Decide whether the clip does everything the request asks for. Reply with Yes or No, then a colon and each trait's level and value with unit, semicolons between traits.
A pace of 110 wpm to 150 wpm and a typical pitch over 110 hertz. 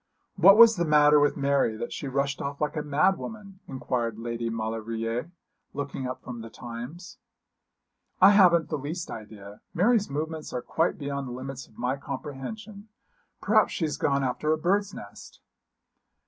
No: average, 165 wpm; medium, 140 Hz